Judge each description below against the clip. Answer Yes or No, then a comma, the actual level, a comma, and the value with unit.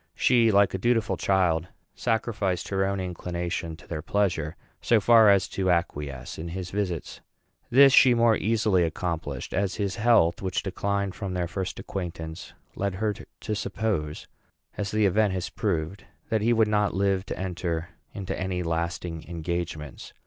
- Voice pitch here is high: No, very low, 95 Hz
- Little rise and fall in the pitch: No, average, 3.5 semitones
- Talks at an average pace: Yes, average, 160 wpm